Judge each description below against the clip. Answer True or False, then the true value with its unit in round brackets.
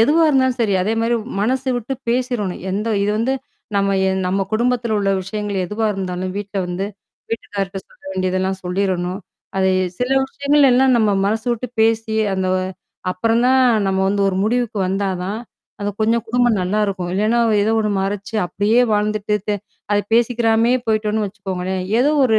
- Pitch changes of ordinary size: True (3.4 semitones)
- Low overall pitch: False (215 Hz)